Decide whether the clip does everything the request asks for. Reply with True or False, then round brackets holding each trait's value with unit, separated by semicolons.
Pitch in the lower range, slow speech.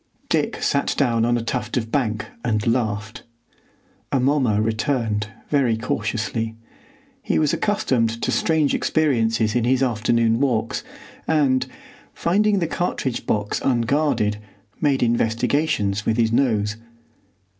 True (120 Hz; 120 wpm)